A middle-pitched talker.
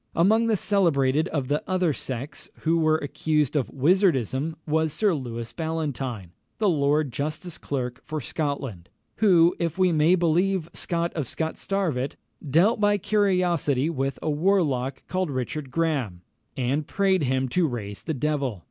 Yes: medium, 155 Hz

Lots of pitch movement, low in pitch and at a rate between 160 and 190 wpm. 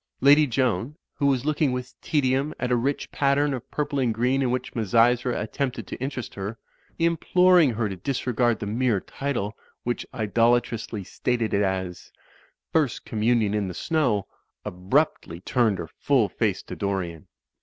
No: average, 4.4 semitones; low, 120 Hz; average, 165 wpm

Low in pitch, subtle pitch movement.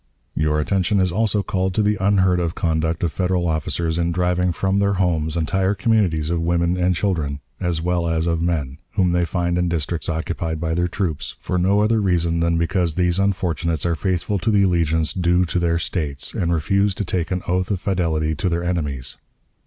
Yes: very low, 85 Hz; narrow, 2.3 semitones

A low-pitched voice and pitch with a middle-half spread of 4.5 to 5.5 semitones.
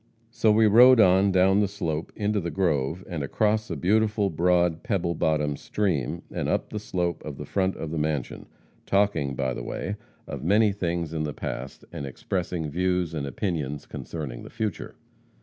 Yes: very low, 90 Hz; average, 4.9 semitones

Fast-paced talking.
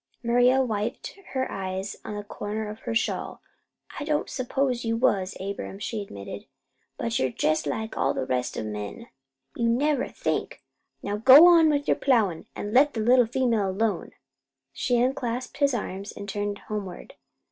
No: average, 175 wpm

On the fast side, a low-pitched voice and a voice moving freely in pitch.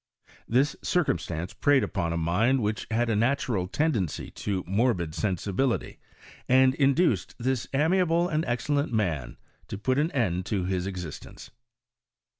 No: slow, 135 wpm; low, 115 Hz; wide, 6.9 semitones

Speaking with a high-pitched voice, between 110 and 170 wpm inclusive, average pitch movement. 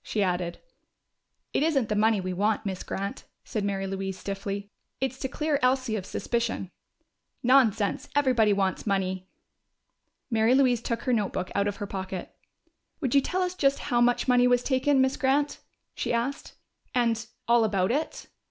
Yes: high, 230 Hz; average, 165 wpm; average, 4.8 semitones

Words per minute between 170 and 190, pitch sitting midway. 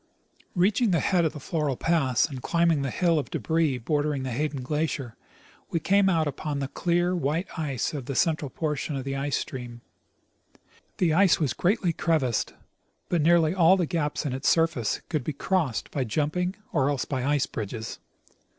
Yes: average, 180 wpm; medium, 150 Hz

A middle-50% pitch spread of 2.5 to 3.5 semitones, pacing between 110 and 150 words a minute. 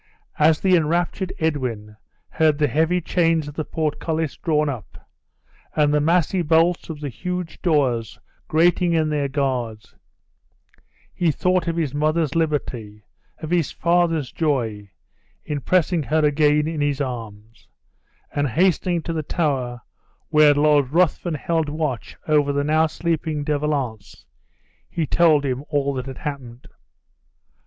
Yes: average, 3.0 semitones; average, 140 wpm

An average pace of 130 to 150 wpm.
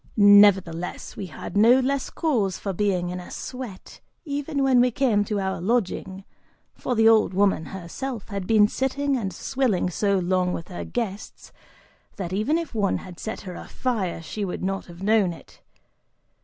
No: average, 170 wpm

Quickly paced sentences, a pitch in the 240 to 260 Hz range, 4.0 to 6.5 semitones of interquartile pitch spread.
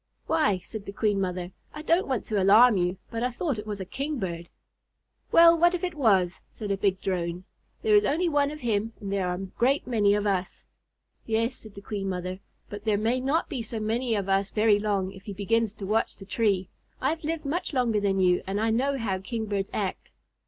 No: fast, 225 wpm; high, 215 Hz; average, 4.7 semitones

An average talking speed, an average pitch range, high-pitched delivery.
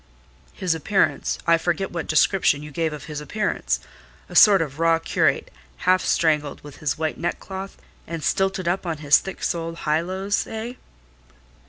No: average, 155 wpm; average, 3.8 semitones; medium, 165 Hz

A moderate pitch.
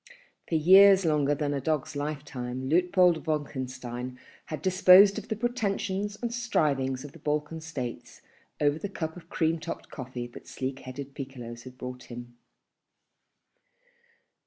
Yes: medium, 150 Hz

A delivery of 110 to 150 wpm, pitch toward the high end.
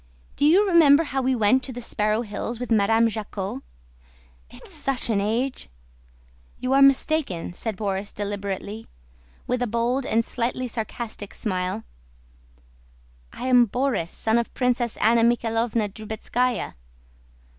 Yes: slow, 135 wpm; high, 230 Hz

